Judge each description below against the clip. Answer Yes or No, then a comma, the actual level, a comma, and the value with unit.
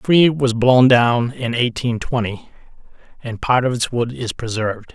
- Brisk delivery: No, average, 180 wpm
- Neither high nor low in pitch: No, low, 120 Hz